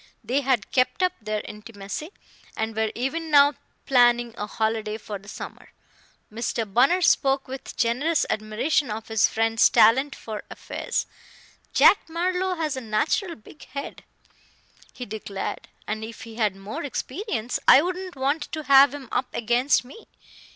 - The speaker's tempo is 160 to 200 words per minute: No, average, 150 wpm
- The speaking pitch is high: Yes, high, 245 Hz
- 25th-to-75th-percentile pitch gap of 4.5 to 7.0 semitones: Yes, average, 4.8 semitones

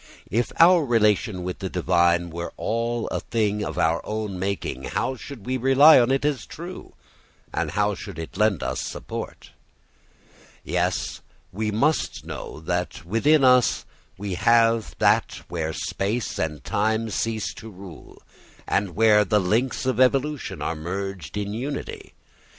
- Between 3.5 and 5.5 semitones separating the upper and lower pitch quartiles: Yes, average, 5.2 semitones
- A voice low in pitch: Yes, low, 105 Hz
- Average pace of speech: Yes, average, 150 wpm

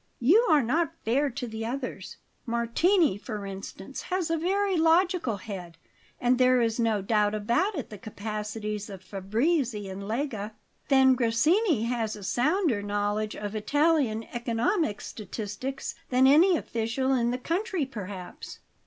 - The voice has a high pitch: Yes, high, 235 Hz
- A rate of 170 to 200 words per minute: No, average, 140 wpm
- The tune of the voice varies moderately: No, wide, 6.0 semitones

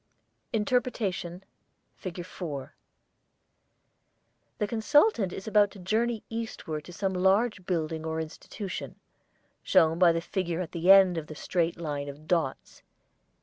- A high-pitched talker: No, medium, 180 Hz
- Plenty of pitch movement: No, average, 4.0 semitones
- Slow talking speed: Yes, slow, 130 wpm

